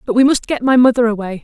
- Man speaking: No, female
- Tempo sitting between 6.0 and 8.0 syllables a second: Yes, 6.9 syllables/s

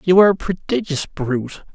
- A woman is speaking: No, male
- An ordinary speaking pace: Yes, average, 170 wpm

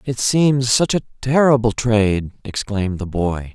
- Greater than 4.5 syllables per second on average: No, 4.4 syllables/s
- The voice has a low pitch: Yes, low, 115 Hz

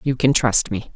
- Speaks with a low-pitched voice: Yes, low, 120 Hz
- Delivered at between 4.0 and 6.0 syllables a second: Yes, 4.7 syllables/s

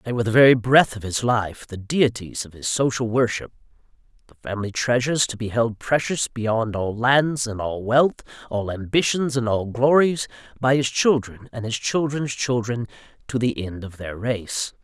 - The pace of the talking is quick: No, average, 180 wpm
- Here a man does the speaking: Yes, male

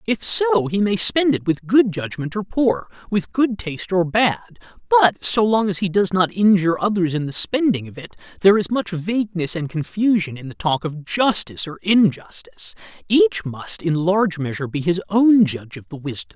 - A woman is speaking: No, male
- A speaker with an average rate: No, fast, 210 wpm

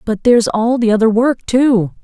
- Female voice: Yes, female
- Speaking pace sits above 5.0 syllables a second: No, 4.8 syllables/s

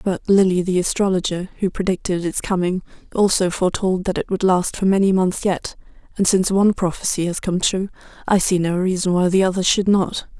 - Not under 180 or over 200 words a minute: Yes, average, 195 wpm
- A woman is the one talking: Yes, female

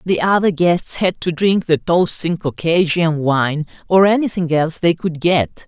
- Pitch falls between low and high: Yes, medium, 170 Hz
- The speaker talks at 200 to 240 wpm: No, average, 180 wpm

